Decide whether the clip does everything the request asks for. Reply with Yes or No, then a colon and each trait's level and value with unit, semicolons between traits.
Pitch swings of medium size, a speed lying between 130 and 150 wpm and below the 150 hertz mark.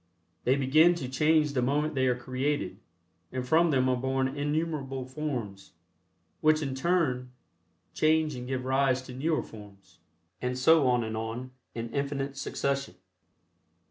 Yes: average, 3.0 semitones; average, 145 wpm; low, 135 Hz